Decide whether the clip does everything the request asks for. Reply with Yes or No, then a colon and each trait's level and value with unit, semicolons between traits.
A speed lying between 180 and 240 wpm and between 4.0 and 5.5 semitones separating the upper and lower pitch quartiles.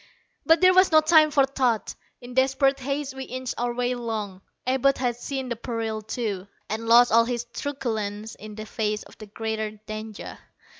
No: average, 185 wpm; average, 3.5 semitones